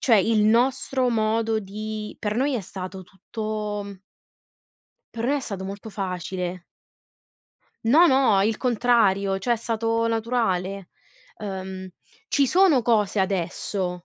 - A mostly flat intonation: No, average, 3.3 semitones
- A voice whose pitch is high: Yes, high, 215 Hz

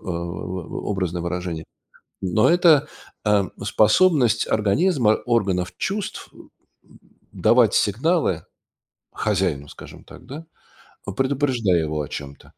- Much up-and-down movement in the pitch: Yes, wide, 7.1 semitones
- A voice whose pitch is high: No, low, 100 Hz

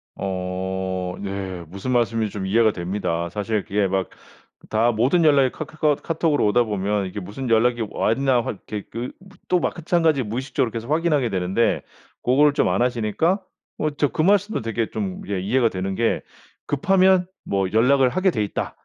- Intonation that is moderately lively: No, wide, 6.3 semitones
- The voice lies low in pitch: Yes, low, 115 Hz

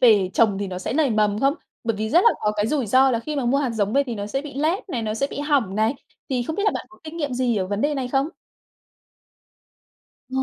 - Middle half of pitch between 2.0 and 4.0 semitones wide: No, average, 5.1 semitones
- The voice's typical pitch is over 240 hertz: Yes, very high, 250 Hz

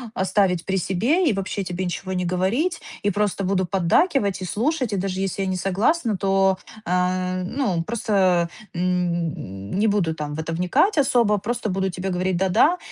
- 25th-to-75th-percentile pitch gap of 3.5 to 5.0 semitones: No, narrow, 2.5 semitones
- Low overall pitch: No, high, 190 Hz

